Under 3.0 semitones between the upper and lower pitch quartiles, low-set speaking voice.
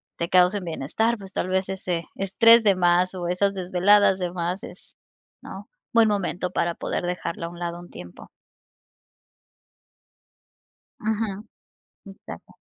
No: narrow, 2.4 semitones; medium, 185 Hz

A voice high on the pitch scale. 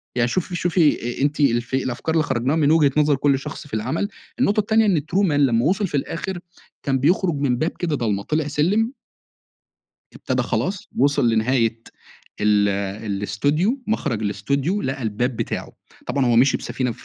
No: medium, 140 Hz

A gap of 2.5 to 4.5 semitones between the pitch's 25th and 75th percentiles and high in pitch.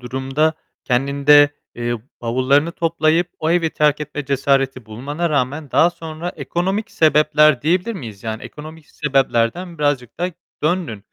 No: average, 3.7 semitones; medium, 150 Hz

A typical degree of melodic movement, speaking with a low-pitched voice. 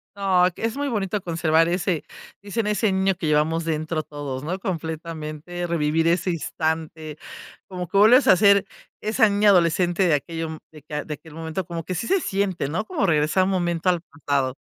No: average, 3.5 semitones; medium, 170 Hz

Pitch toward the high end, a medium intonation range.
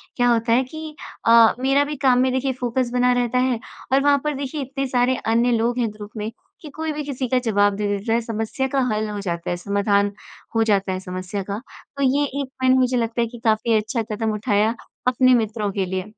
Yes: high, 235 Hz; average, 3.5 semitones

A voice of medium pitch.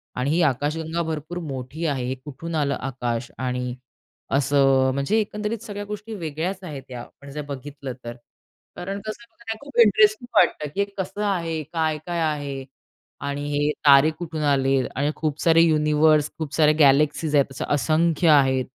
Yes: medium, 150 Hz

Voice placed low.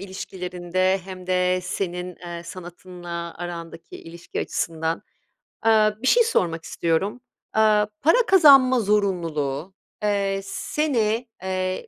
No: medium, 185 Hz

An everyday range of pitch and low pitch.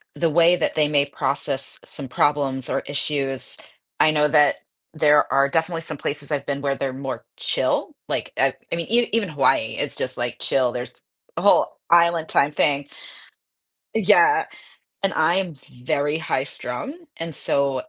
No: average, 3.2 semitones; medium, 145 Hz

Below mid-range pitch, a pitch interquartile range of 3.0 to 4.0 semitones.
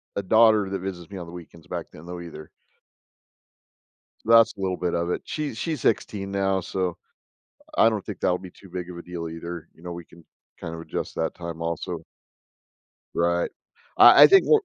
No: very low, 90 Hz; narrow, 2.6 semitones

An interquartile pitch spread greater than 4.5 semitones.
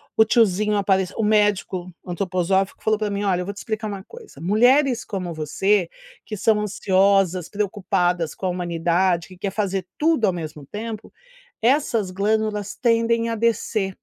No: average, 3.0 semitones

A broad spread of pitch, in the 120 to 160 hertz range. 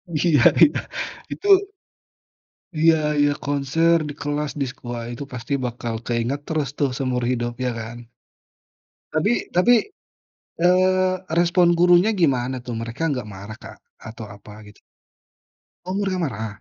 Yes: wide, 6.4 semitones; medium, 140 Hz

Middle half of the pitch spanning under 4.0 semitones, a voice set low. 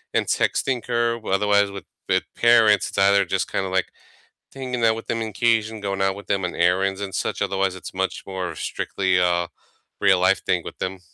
Yes: average, 2.9 semitones; very low, 95 Hz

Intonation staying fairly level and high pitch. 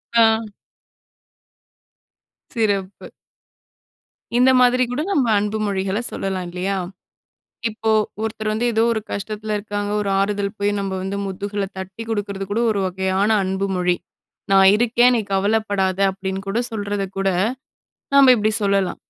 Yes: narrow, 2.2 semitones; high, 205 Hz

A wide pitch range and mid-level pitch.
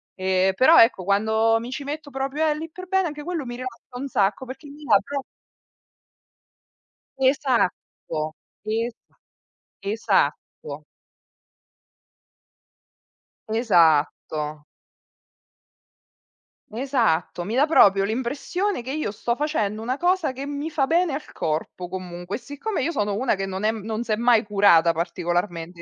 No: wide, 6.7 semitones; high, 230 Hz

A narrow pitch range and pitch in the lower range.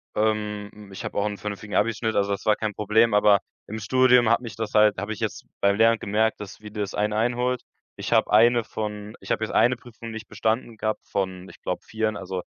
Yes: narrow, 1.6 semitones; low, 105 Hz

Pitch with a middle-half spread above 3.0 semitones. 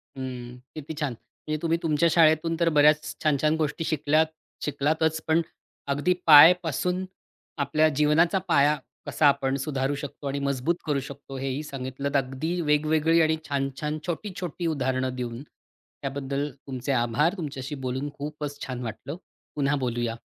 No: average, 2.7 semitones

